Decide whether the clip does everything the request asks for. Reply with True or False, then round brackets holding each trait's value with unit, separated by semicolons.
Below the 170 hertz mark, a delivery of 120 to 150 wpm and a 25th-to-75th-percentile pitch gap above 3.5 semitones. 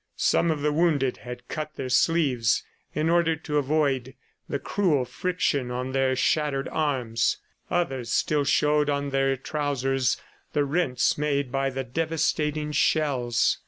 False (140 Hz; 140 wpm; 2.7 semitones)